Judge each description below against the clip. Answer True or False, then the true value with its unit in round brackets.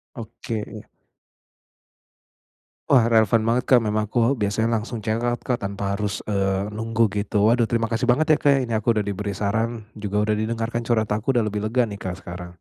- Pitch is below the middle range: True (110 Hz)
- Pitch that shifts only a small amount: True (2.1 semitones)